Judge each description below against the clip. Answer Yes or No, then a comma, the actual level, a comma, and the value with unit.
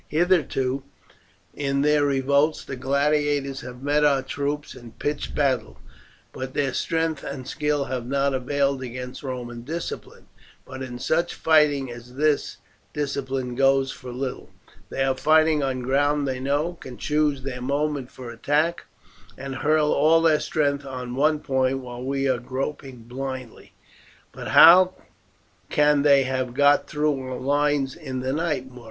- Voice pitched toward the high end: No, medium, 140 Hz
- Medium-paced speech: Yes, average, 150 wpm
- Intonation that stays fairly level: Yes, narrow, 2.3 semitones